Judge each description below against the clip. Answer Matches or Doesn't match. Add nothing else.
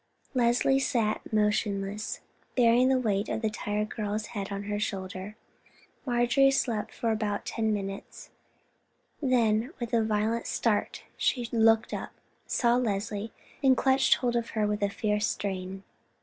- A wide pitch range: Doesn't match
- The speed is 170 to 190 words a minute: Doesn't match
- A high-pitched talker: Matches